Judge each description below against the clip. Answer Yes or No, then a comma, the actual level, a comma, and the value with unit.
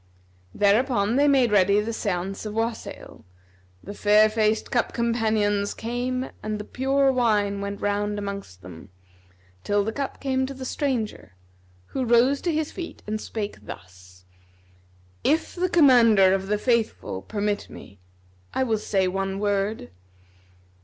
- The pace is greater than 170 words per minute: No, average, 145 wpm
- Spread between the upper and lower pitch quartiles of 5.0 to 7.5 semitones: No, average, 3.7 semitones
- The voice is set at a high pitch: Yes, high, 215 Hz